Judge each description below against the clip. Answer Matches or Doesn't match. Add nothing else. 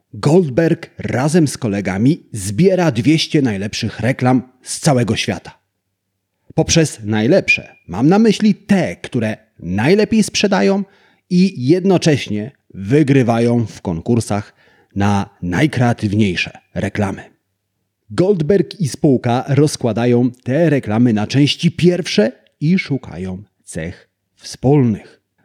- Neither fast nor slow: Doesn't match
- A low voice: Matches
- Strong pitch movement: Matches